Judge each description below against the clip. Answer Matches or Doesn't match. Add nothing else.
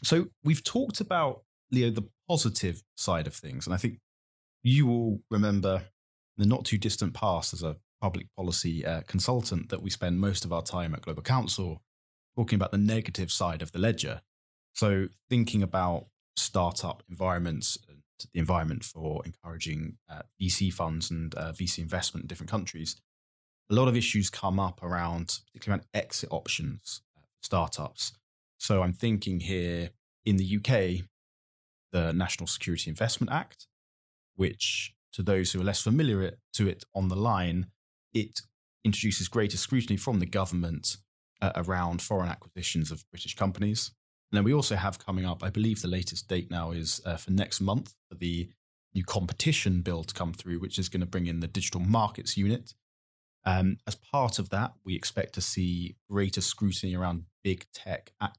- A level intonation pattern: Doesn't match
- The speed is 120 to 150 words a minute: Doesn't match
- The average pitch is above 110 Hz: Doesn't match